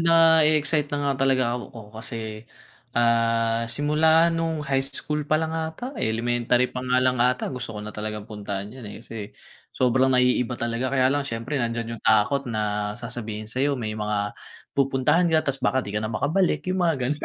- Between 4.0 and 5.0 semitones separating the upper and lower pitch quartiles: Yes, average, 4.3 semitones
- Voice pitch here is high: No, low, 125 Hz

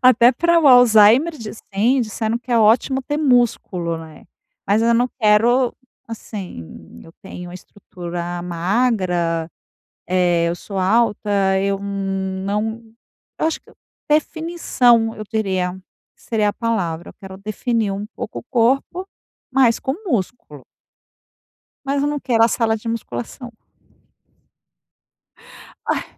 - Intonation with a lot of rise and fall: No, average, 4.3 semitones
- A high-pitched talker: Yes, high, 220 Hz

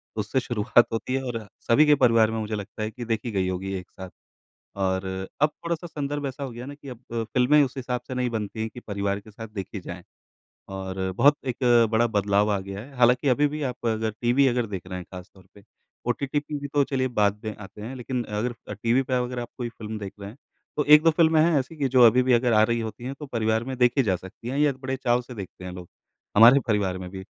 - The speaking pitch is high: No, low, 120 Hz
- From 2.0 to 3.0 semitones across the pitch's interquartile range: No, average, 4.2 semitones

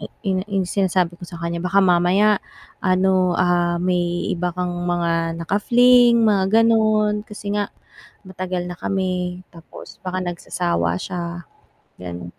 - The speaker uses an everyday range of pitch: No, narrow, 2.3 semitones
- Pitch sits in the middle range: Yes, medium, 180 Hz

